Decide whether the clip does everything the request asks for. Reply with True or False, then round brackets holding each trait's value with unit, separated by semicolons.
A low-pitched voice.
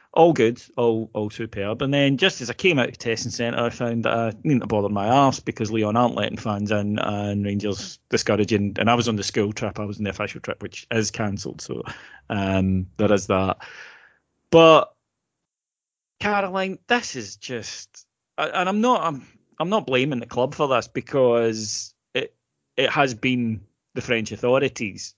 True (115 Hz)